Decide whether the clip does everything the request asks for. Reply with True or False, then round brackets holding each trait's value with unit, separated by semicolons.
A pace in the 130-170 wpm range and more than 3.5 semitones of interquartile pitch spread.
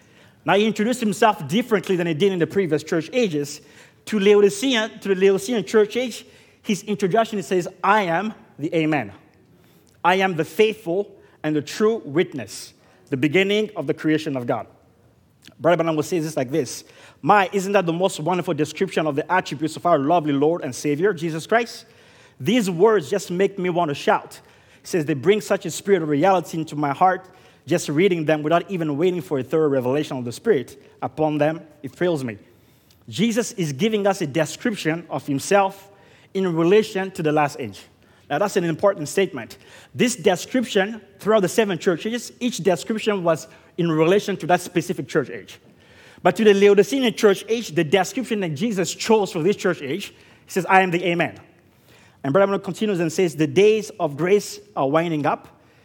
False (185 wpm; 4.8 semitones)